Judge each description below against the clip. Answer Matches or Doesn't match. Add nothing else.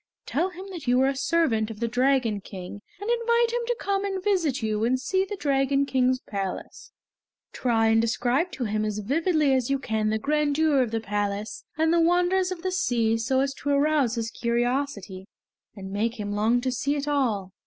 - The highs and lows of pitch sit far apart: Matches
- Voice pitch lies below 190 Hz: Doesn't match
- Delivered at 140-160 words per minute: Doesn't match